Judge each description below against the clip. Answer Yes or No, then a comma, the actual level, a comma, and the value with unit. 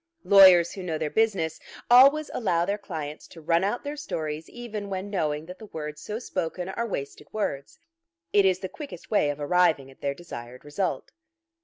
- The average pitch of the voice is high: No, medium, 180 Hz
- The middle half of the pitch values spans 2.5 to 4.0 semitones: No, average, 5.2 semitones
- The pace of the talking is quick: No, average, 185 wpm